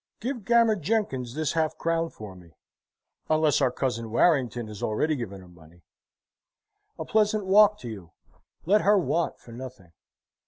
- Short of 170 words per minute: Yes, average, 155 wpm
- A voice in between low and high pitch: Yes, medium, 145 Hz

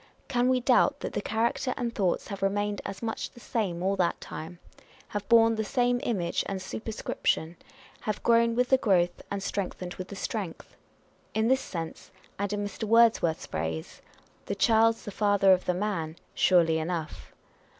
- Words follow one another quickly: No, average, 185 wpm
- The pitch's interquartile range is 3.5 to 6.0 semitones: Yes, average, 4.1 semitones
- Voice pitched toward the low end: No, high, 205 Hz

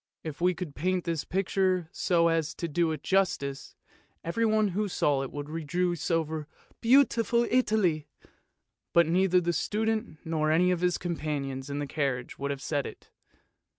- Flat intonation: No, average, 3.7 semitones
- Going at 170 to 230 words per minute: Yes, average, 175 wpm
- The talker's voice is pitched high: No, medium, 170 Hz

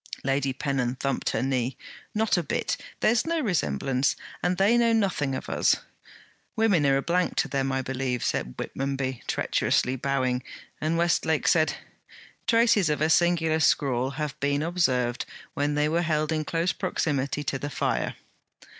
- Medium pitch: Yes, medium, 145 Hz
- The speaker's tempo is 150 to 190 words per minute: Yes, average, 160 wpm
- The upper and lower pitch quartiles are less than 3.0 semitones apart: No, average, 4.5 semitones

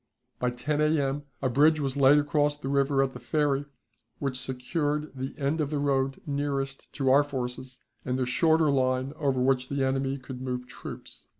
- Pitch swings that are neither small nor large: No, narrow, 2.0 semitones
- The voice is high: No, low, 135 Hz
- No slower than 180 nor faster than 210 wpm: Yes, average, 185 wpm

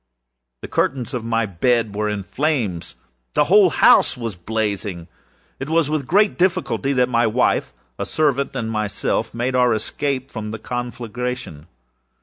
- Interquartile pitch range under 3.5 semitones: No, average, 4.3 semitones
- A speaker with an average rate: Yes, average, 150 wpm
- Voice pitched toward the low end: Yes, low, 120 Hz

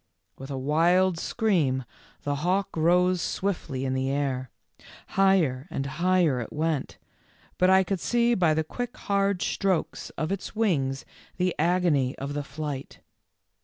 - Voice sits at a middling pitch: Yes, medium, 165 Hz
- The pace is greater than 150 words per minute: No, average, 145 wpm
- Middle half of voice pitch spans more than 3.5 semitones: Yes, average, 5.3 semitones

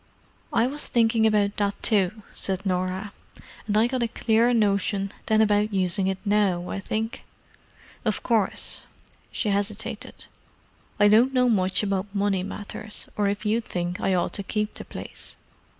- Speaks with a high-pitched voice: Yes, high, 205 Hz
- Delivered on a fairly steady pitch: Yes, narrow, 2.1 semitones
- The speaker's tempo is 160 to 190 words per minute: No, average, 150 wpm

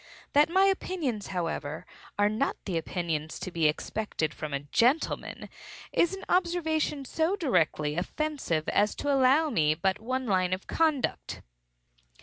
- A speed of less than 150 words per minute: Yes, average, 140 wpm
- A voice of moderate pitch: No, high, 220 Hz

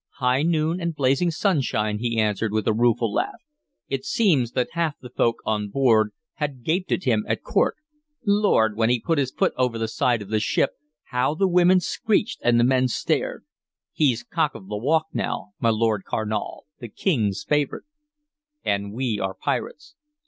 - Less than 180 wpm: No, average, 185 wpm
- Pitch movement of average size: No, wide, 5.8 semitones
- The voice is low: Yes, low, 125 Hz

